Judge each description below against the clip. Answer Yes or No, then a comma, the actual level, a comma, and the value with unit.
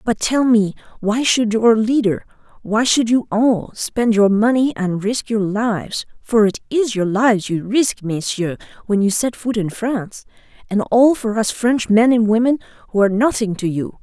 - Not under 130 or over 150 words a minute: No, average, 175 wpm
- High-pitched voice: Yes, high, 220 Hz